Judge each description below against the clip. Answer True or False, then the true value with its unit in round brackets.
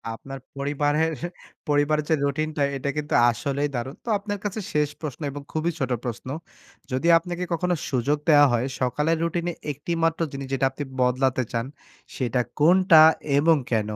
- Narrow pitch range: False (3.4 semitones)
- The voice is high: False (145 Hz)